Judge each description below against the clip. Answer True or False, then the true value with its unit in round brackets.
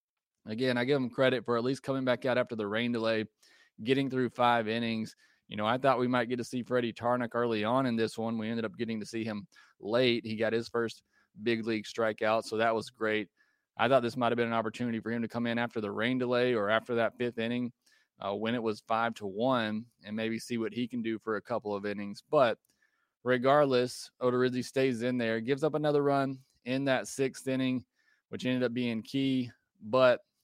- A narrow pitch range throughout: True (2.0 semitones)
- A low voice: True (120 Hz)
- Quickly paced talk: True (225 wpm)